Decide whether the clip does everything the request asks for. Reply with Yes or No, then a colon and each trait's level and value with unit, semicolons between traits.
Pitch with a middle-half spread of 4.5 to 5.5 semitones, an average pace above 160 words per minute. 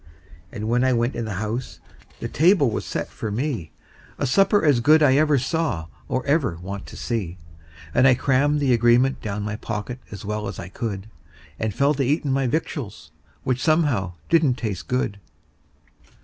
Yes: average, 5.0 semitones; average, 180 wpm